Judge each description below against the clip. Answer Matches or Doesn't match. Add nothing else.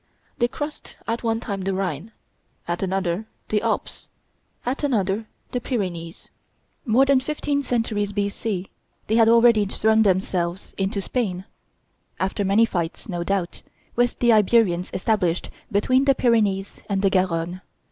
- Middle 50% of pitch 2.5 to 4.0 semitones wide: Matches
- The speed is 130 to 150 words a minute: Matches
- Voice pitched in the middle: Doesn't match